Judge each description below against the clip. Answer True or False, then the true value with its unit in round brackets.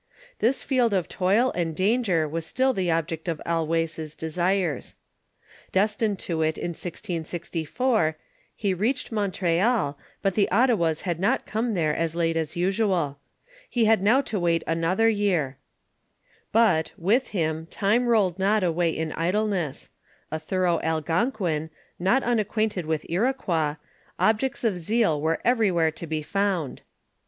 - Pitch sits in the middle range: True (180 Hz)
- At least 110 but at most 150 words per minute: True (140 wpm)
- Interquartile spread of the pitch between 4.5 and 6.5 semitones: True (4.9 semitones)